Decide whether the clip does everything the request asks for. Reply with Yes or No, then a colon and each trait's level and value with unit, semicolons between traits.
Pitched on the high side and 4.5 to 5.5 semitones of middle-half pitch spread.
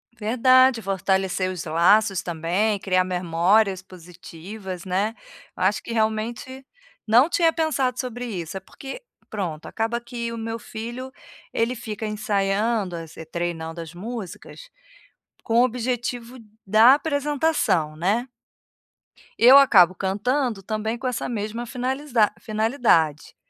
Yes: high, 220 Hz; average, 4.8 semitones